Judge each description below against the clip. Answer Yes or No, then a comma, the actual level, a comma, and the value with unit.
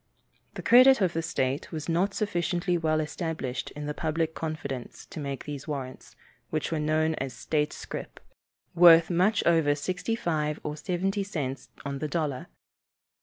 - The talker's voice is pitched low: No, medium, 160 Hz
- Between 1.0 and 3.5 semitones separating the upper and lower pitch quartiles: Yes, average, 2.9 semitones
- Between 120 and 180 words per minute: Yes, average, 160 wpm